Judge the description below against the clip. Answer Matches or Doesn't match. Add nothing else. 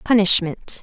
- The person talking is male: Doesn't match